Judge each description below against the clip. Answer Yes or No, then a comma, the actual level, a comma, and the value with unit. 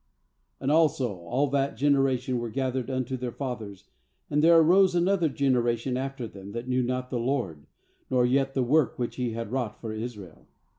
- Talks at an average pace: Yes, average, 180 wpm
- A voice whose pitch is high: No, low, 130 Hz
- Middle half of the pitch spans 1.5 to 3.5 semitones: Yes, narrow, 2.6 semitones